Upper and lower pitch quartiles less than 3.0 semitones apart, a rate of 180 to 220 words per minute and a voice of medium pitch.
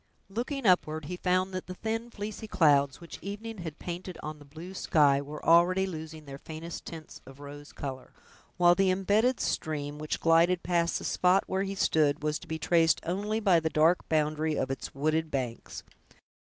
No: average, 3.6 semitones; average, 185 wpm; medium, 165 Hz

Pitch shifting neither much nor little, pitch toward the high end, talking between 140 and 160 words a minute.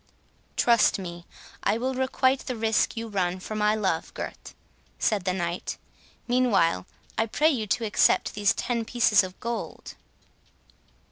Yes: average, 4.1 semitones; high, 215 Hz; average, 145 wpm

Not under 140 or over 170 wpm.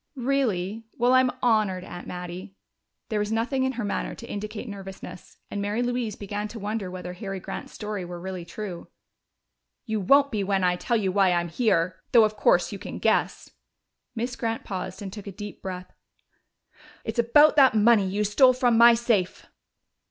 No: average, 185 wpm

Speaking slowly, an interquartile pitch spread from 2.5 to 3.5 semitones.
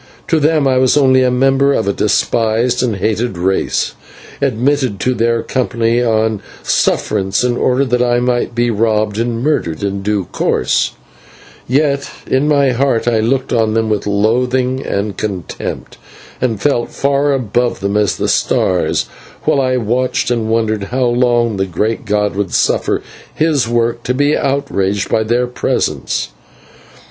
No: average, 155 wpm; average, 3.1 semitones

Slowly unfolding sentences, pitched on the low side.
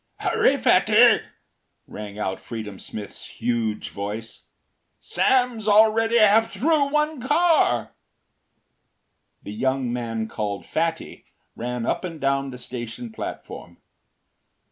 Yes: slow, 105 wpm; low, 130 Hz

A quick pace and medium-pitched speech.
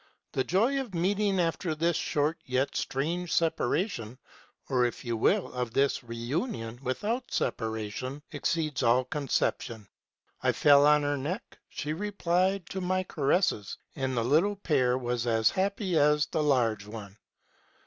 No: average, 150 wpm; medium, 145 Hz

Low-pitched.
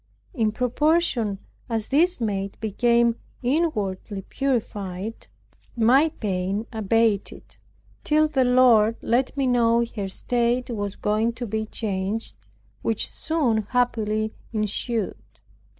No: high, 230 Hz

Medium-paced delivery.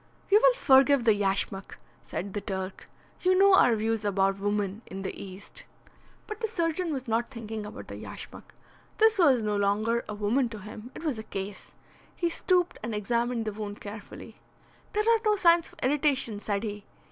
Yes: average, 185 wpm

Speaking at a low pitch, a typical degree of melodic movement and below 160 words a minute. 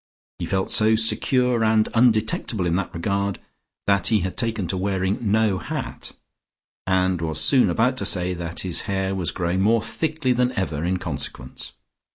No: low, 100 Hz; average, 3.5 semitones; average, 170 wpm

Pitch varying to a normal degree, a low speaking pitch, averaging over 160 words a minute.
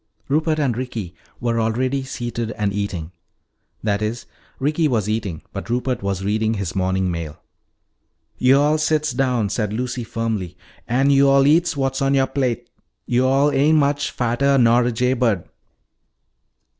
No: average, 4.2 semitones; low, 120 Hz; average, 145 wpm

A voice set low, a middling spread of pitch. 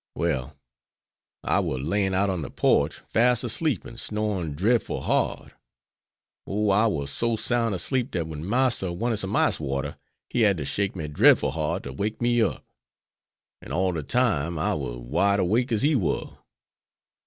No: low, 100 Hz; wide, 6.4 semitones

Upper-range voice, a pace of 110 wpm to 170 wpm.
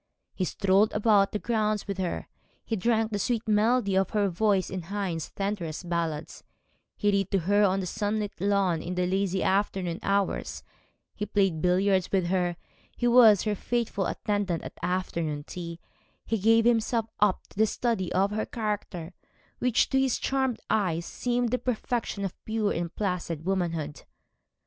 Yes: high, 200 Hz; average, 165 wpm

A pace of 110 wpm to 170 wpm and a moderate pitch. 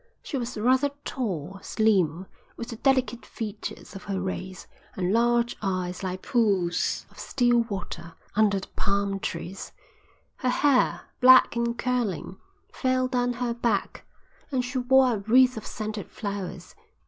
No: average, 145 wpm; high, 220 Hz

